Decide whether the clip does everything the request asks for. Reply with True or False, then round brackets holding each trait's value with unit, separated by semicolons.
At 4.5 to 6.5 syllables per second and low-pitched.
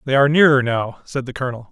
False (7.2 syllables/s; 130 Hz)